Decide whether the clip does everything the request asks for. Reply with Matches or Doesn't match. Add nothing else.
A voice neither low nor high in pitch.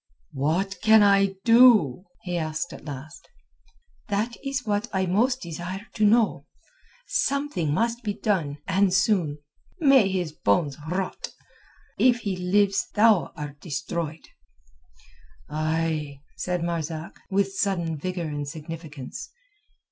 Matches